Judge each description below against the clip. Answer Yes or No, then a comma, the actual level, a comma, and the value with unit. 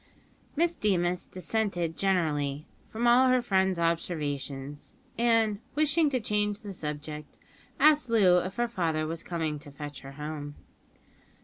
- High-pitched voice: No, medium, 180 Hz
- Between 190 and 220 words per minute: No, slow, 135 wpm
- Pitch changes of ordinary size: No, wide, 7.0 semitones